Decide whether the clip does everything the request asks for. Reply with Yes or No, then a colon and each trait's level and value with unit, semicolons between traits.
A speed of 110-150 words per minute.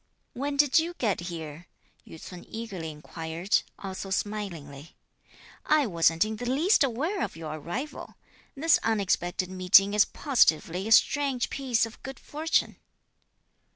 Yes: slow, 135 wpm